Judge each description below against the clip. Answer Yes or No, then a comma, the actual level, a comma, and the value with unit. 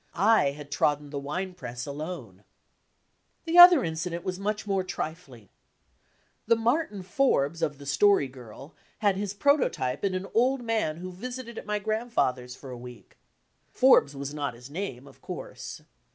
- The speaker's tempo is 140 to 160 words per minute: Yes, average, 155 wpm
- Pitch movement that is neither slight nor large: No, wide, 7.5 semitones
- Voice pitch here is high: No, medium, 180 Hz